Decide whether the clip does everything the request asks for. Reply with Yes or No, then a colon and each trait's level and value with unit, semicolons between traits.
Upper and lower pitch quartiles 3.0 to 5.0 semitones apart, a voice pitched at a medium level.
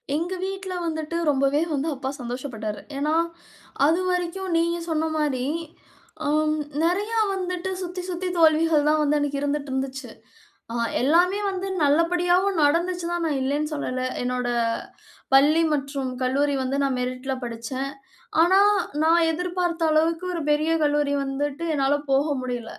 No: average, 4.2 semitones; very high, 305 Hz